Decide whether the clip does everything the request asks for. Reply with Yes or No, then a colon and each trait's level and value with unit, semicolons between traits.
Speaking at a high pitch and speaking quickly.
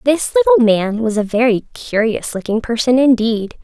No: high, 240 Hz; average, 165 wpm